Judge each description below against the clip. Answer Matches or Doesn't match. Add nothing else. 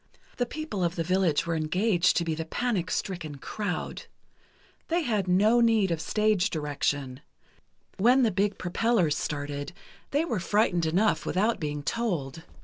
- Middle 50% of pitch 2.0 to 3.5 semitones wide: Doesn't match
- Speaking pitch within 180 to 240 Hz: Matches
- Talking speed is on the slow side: Doesn't match